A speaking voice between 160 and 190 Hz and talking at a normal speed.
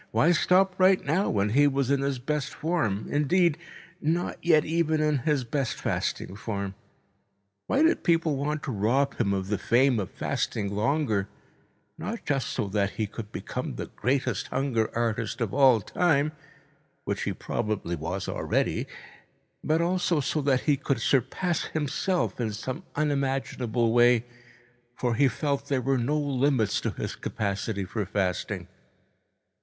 No: low, 135 Hz; average, 155 wpm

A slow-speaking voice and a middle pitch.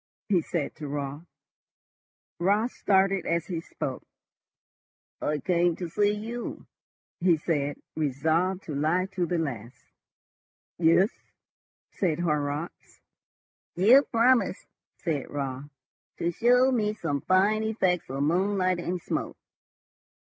Yes: slow, 115 wpm; medium, 175 Hz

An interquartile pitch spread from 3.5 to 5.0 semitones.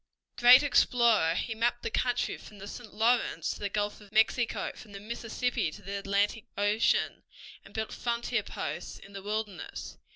No: average, 2.9 semitones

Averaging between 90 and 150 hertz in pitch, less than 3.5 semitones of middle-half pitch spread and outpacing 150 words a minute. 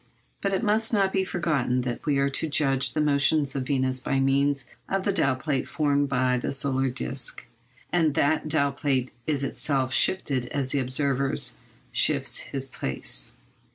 Yes: medium, 140 Hz; average, 2.7 semitones; average, 170 wpm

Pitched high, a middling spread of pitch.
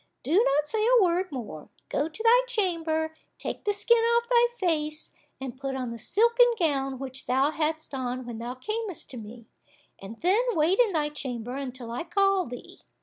No: very high, 310 Hz; wide, 7.8 semitones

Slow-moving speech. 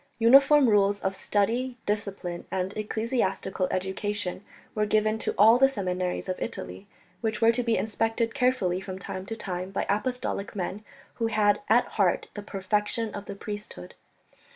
No: average, 155 wpm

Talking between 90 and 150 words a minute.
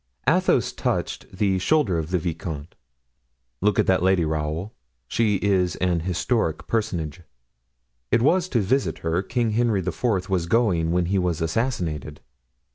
Yes: average, 145 wpm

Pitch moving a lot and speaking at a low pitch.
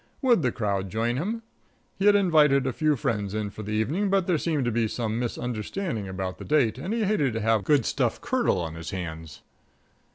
Yes: wide, 7.8 semitones; low, 120 Hz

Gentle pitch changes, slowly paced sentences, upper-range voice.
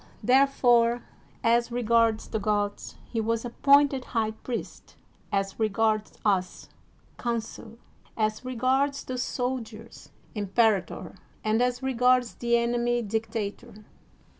Yes: narrow, 2.3 semitones; slow, 115 wpm; high, 230 Hz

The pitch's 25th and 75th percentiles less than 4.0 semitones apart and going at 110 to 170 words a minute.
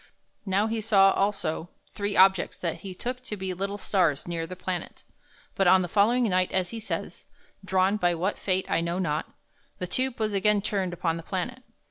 No: narrow, 2.6 semitones; average, 195 wpm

